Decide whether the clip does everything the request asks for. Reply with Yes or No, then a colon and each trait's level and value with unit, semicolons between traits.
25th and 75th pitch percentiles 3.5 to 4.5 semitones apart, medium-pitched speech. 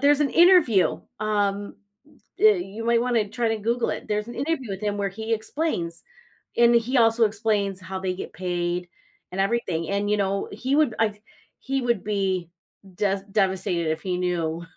No: average, 3.8 semitones; high, 205 Hz